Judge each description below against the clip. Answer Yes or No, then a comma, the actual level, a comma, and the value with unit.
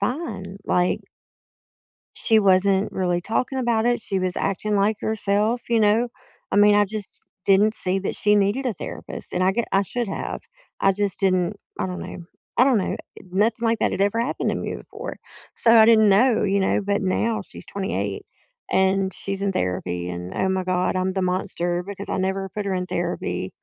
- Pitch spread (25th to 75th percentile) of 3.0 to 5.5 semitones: No, narrow, 2.6 semitones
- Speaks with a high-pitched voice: Yes, high, 200 Hz